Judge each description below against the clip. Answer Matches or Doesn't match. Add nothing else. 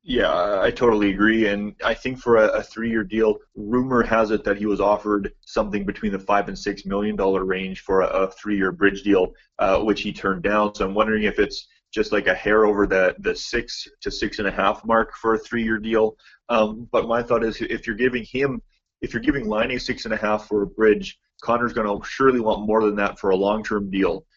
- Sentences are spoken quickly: Matches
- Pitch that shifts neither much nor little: Doesn't match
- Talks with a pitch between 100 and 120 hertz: Matches